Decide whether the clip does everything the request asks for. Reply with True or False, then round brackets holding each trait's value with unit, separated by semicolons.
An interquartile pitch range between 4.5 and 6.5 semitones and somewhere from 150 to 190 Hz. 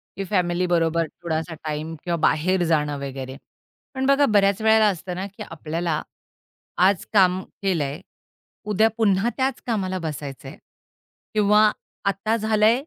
True (4.8 semitones; 185 Hz)